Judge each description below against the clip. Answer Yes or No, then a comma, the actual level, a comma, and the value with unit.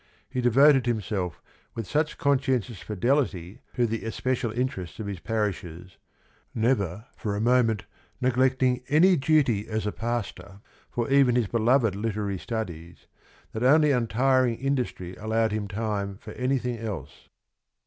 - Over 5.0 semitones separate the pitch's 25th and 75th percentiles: No, average, 4.0 semitones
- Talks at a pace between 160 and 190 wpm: No, slow, 135 wpm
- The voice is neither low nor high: No, low, 115 Hz